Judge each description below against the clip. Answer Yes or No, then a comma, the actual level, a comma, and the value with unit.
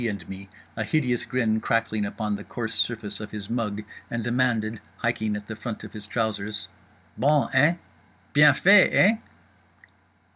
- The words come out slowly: No, average, 150 wpm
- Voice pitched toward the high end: No, low, 110 Hz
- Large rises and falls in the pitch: No, average, 2.9 semitones